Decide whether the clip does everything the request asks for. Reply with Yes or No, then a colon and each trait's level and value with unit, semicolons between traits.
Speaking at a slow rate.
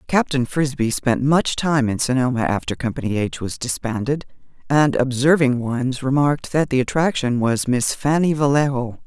No: average, 150 wpm